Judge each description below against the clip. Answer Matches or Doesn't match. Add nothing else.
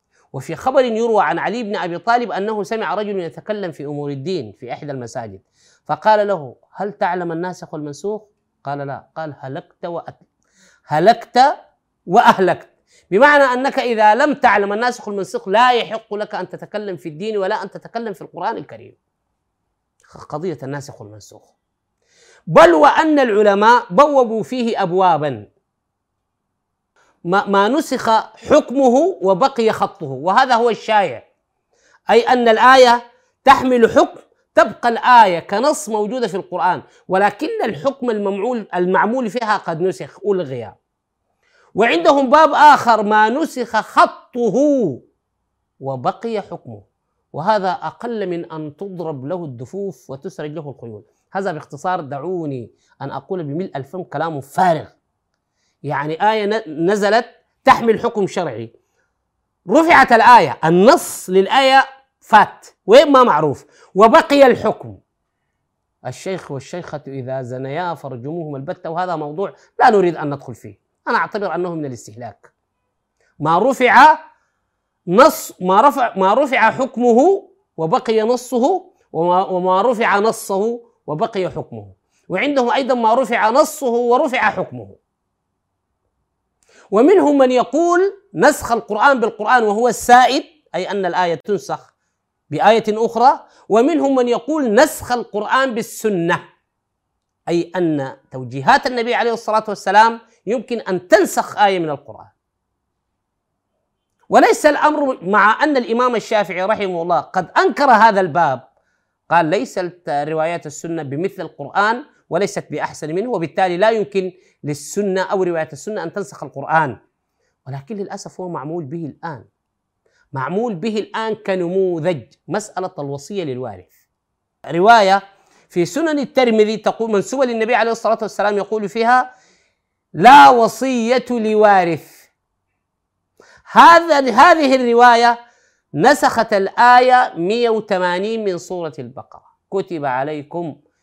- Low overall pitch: Doesn't match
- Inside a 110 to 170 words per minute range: Matches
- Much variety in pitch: Matches